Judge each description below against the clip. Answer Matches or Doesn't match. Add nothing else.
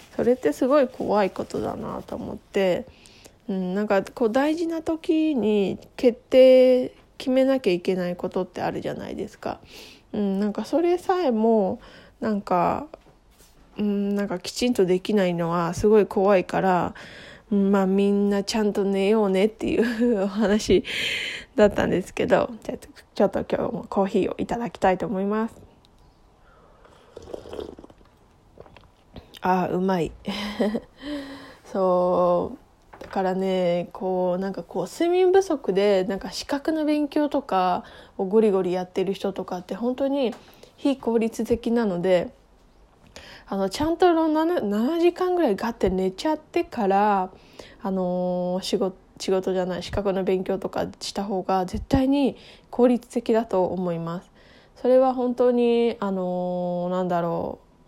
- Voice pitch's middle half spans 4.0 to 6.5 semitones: Matches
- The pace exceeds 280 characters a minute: Doesn't match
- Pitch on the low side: Doesn't match